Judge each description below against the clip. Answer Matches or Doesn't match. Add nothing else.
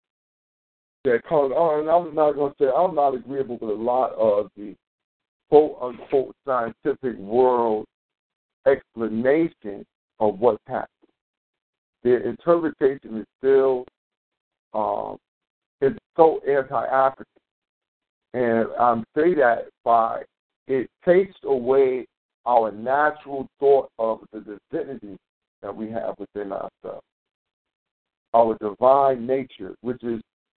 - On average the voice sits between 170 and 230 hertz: Doesn't match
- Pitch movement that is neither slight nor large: Matches